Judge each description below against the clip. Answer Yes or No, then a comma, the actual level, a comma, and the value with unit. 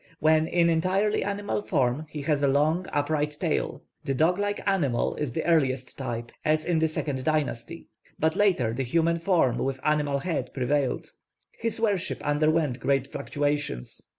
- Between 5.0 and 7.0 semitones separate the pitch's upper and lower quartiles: No, average, 3.6 semitones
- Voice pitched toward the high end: No, medium, 155 Hz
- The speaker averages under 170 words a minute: Yes, average, 160 wpm